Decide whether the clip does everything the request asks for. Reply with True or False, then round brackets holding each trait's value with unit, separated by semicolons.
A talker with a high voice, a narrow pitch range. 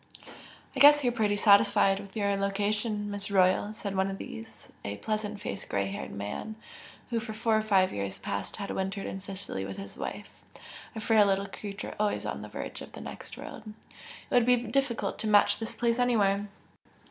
True (205 Hz; 2.2 semitones)